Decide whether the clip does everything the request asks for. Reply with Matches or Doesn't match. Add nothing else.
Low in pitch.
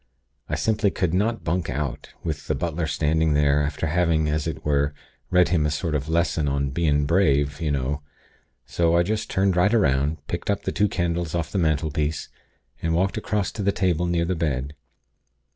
Matches